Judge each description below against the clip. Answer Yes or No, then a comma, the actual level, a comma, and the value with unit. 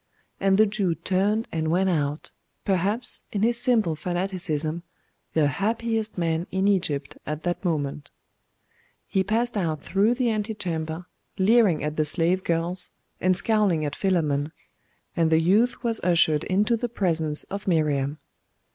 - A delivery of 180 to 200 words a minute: No, average, 145 wpm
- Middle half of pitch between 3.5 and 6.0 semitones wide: Yes, average, 4.7 semitones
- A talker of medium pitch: Yes, medium, 180 Hz